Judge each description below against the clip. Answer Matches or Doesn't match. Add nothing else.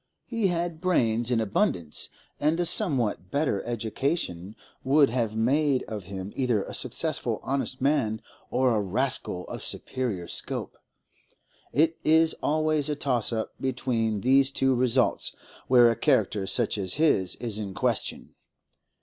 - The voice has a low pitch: Matches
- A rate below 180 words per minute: Matches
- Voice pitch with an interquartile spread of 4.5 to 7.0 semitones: Matches